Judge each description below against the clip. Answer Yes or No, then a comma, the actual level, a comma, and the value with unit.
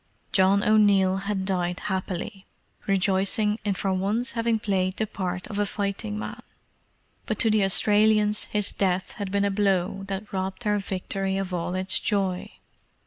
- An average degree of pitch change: No, narrow, 1.8 semitones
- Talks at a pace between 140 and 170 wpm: Yes, average, 160 wpm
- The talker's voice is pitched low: No, high, 195 Hz